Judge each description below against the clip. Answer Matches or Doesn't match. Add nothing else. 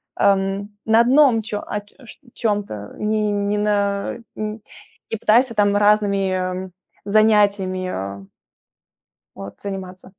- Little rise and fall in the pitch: Matches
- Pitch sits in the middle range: Doesn't match